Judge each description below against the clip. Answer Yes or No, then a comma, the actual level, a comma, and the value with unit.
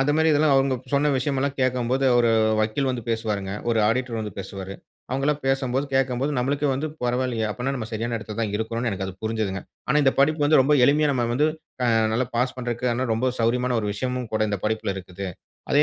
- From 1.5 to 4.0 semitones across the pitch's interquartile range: Yes, average, 3.4 semitones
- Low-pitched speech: Yes, low, 125 Hz